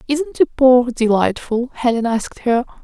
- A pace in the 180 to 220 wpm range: No, slow, 125 wpm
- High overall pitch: Yes, very high, 250 Hz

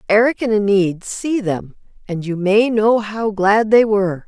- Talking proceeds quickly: No, average, 180 wpm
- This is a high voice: Yes, high, 205 Hz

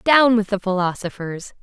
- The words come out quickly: No, average, 150 wpm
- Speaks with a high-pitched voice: Yes, high, 205 Hz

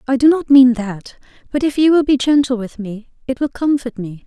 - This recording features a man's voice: No, female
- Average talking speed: No, fast, 240 wpm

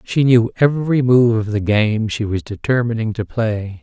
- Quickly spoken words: No, average, 190 wpm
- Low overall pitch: Yes, low, 115 Hz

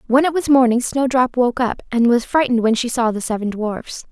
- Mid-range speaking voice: No, high, 245 Hz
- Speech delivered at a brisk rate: Yes, fast, 235 wpm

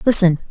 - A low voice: No, high, 190 Hz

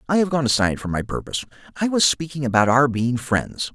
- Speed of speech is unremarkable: No, fast, 225 wpm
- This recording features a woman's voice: No, male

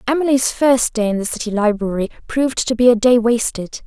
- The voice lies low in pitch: No, high, 235 Hz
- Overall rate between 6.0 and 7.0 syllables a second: No, 5.7 syllables/s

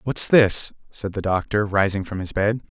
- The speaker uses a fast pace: No, average, 195 wpm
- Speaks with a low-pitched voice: Yes, low, 100 Hz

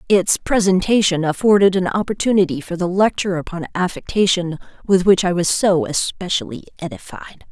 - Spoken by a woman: Yes, female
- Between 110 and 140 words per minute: Yes, slow, 135 wpm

